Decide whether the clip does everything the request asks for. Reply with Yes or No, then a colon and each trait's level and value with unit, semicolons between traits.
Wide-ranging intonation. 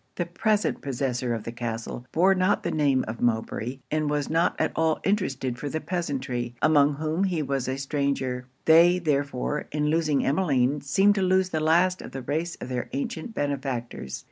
No: average, 4.4 semitones